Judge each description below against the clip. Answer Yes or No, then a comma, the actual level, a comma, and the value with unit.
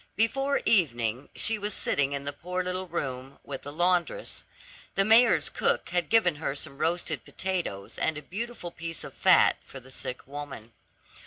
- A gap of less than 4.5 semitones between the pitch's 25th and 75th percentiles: No, wide, 5.4 semitones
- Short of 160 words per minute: No, average, 170 wpm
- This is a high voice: No, medium, 165 Hz